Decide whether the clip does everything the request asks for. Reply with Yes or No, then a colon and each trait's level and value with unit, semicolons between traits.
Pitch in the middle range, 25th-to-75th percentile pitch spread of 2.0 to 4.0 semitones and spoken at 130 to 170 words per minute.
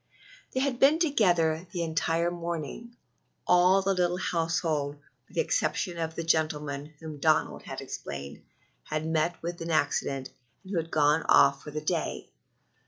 Yes: medium, 165 Hz; narrow, 2.5 semitones; average, 160 wpm